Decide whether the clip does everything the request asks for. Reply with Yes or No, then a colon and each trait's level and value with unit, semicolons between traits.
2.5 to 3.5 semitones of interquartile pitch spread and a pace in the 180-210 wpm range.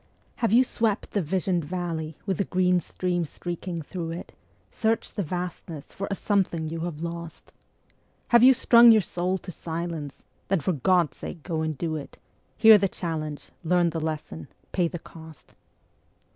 No: average, 2.9 semitones; average, 170 wpm